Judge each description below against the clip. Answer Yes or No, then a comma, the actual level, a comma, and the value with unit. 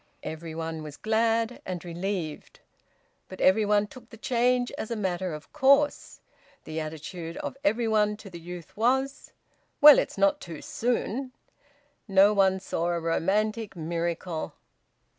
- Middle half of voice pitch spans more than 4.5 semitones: Yes, average, 5.1 semitones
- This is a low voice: No, high, 195 Hz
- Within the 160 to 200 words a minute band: No, average, 145 wpm